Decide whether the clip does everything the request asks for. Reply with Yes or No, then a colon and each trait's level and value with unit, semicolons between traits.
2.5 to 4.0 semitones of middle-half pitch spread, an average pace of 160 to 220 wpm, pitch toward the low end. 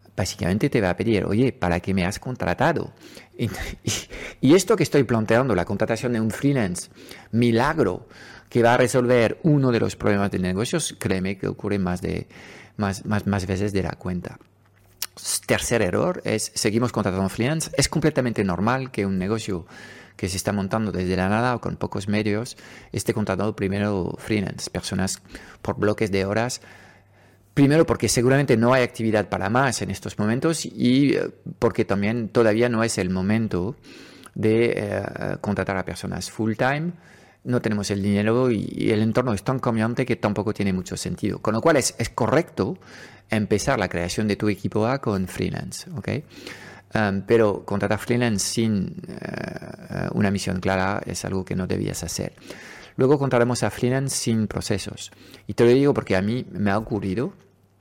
Yes: average, 3.7 semitones; average, 175 wpm; low, 110 Hz